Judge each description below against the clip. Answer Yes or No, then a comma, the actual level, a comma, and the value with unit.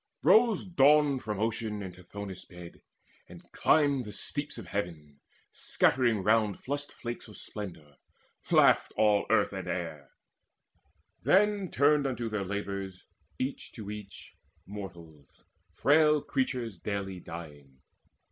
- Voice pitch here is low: Yes, low, 105 Hz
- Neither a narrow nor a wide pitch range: No, wide, 6.7 semitones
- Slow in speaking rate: Yes, slow, 120 wpm